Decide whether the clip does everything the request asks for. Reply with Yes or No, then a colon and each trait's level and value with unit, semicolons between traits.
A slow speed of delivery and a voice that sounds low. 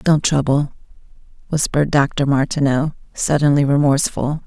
No: slow, 95 wpm; medium, 145 Hz